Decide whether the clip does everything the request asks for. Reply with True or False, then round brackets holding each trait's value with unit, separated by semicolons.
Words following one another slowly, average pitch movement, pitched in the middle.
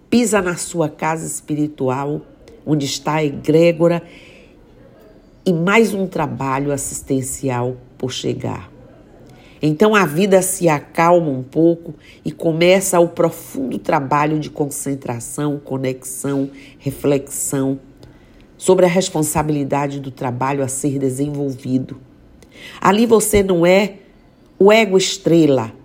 True (105 wpm; 4.2 semitones; 150 Hz)